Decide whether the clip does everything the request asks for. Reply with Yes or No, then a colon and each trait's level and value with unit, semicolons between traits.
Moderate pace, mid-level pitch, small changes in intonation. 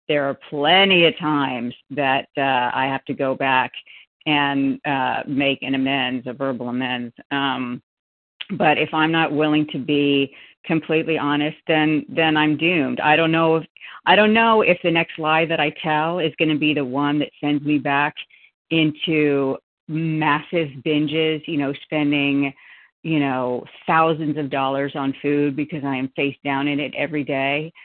Yes: average, 170 wpm; medium, 145 Hz; narrow, 2.3 semitones